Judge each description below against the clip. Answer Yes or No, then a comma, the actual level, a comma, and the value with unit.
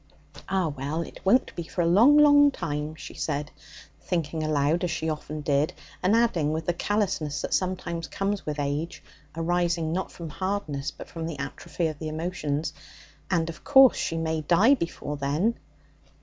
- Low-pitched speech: No, medium, 165 Hz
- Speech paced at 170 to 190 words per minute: Yes, average, 175 wpm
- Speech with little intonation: No, average, 3.5 semitones